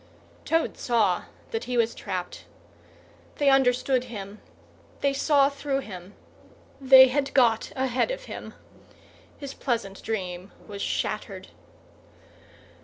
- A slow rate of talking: Yes, slow, 110 wpm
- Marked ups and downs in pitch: No, average, 4.9 semitones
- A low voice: No, very high, 250 Hz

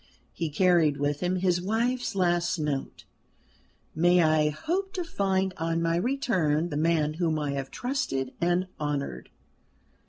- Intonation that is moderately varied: Yes, average, 3.8 semitones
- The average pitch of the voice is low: No, medium, 170 Hz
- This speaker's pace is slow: No, average, 145 wpm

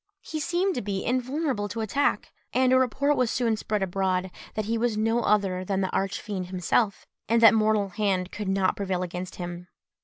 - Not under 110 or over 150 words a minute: No, average, 195 wpm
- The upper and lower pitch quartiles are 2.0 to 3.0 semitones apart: No, average, 4.1 semitones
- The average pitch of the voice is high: Yes, high, 210 Hz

